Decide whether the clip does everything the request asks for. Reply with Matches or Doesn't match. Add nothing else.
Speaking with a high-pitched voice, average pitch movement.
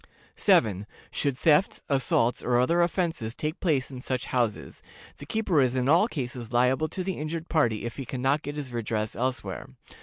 Doesn't match